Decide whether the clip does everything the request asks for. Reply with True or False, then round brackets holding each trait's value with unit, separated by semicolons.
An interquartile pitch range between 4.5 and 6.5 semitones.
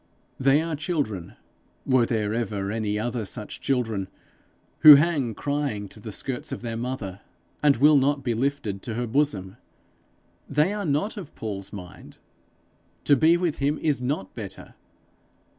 True (5.4 semitones)